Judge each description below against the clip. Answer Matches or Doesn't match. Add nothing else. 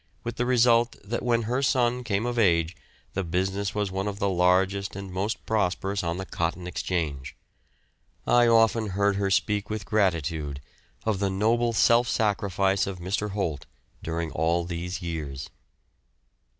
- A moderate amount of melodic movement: Matches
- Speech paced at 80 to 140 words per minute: Doesn't match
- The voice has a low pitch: Matches